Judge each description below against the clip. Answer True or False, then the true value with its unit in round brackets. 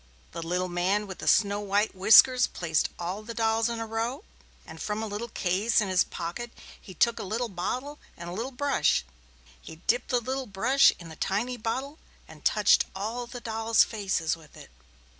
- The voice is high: True (215 Hz)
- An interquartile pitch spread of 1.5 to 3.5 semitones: False (4.4 semitones)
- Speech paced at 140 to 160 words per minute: False (195 wpm)